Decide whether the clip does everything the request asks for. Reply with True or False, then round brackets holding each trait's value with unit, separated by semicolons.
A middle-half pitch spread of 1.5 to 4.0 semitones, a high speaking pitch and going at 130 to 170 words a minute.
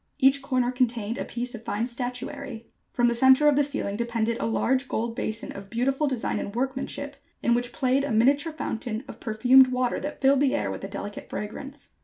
False (2.9 semitones; 250 Hz; 205 wpm)